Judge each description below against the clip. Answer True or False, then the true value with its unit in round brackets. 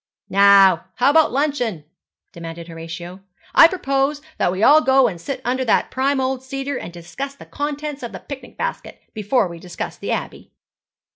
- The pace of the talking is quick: False (170 wpm)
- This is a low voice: False (255 Hz)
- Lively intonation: True (7.4 semitones)